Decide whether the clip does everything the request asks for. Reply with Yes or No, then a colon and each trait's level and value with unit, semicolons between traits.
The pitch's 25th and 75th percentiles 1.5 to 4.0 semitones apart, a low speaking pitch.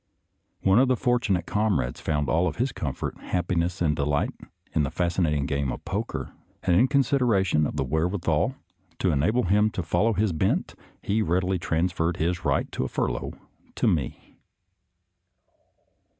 No: average, 5.1 semitones; very low, 90 Hz